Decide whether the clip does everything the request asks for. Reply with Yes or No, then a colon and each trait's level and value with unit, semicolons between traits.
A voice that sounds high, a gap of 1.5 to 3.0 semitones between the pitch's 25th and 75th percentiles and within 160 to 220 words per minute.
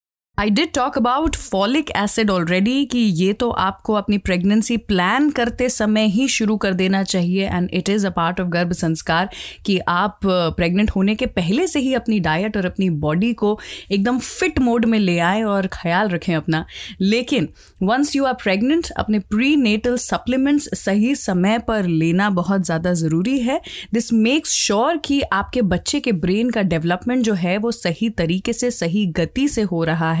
No: high, 210 Hz; average, 4.9 semitones; average, 185 wpm